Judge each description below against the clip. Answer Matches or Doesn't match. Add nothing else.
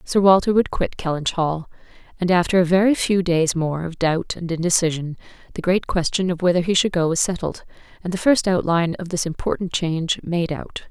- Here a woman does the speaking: Matches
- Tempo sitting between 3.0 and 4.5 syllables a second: Doesn't match